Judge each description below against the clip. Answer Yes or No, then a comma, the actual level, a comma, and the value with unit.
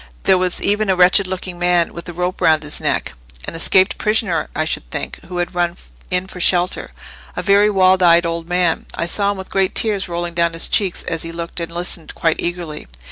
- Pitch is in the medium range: Yes, medium, 175 Hz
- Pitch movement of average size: No, narrow, 2.0 semitones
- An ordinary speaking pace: No, fast, 210 wpm